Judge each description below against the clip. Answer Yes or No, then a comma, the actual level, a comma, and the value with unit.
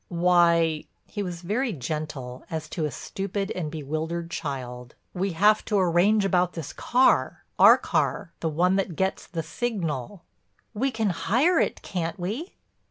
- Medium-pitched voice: Yes, medium, 175 Hz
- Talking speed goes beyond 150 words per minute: No, average, 145 wpm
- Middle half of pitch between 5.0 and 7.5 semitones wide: No, average, 4.2 semitones